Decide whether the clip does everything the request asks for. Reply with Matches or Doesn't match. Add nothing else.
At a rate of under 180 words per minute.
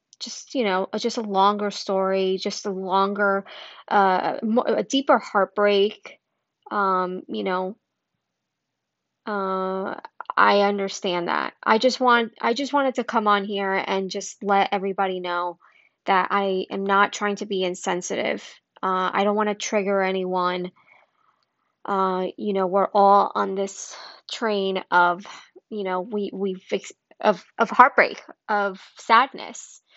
Matches